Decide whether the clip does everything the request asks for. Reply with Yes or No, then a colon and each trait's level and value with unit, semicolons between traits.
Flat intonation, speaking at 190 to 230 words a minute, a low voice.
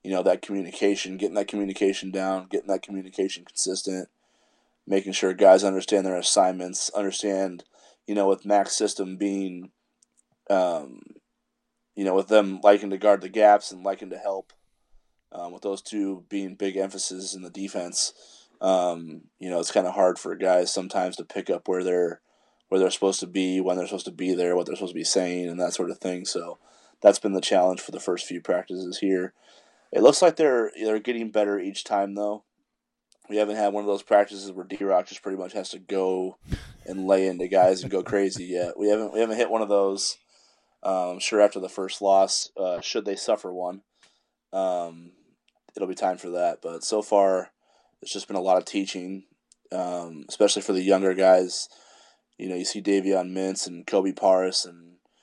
Yes: narrow, 1.4 semitones; average, 200 wpm; very low, 95 Hz